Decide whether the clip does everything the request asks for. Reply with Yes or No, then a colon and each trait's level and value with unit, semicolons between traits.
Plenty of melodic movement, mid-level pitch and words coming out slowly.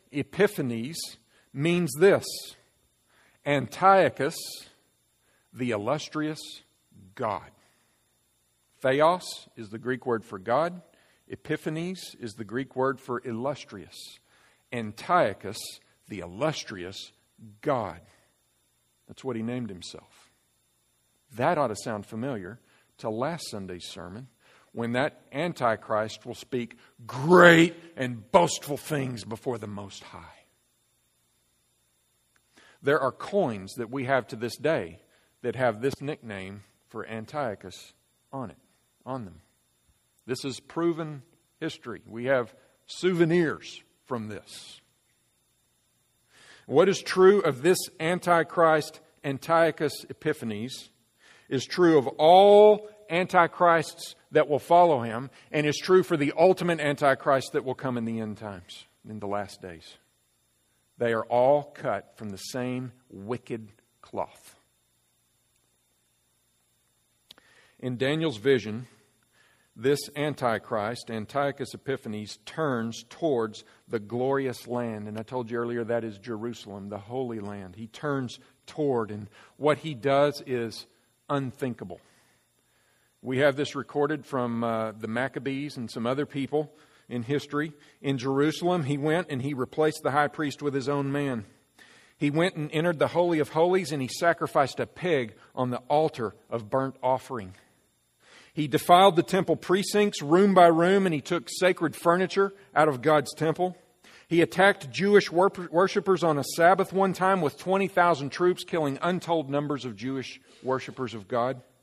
No: wide, 5.8 semitones; low, 130 Hz; slow, 130 wpm